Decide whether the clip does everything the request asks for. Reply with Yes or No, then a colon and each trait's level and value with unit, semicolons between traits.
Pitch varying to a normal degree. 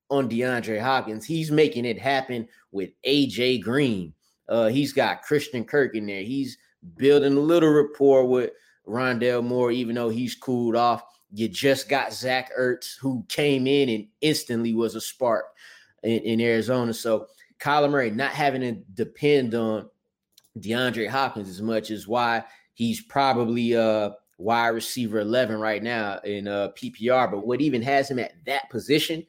Yes: average, 3.5 semitones